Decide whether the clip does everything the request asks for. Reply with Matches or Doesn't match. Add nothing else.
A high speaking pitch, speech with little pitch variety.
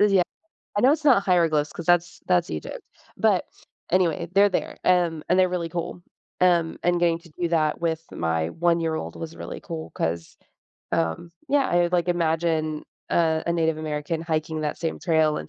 Doesn't match